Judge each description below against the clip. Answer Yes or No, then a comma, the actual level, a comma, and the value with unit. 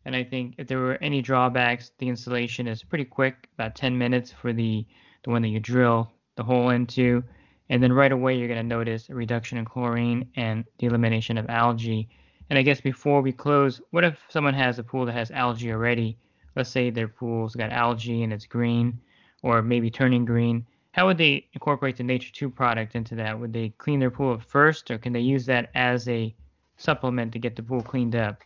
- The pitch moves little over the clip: Yes, narrow, 2.0 semitones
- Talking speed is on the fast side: Yes, fast, 215 wpm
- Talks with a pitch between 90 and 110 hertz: No, low, 120 Hz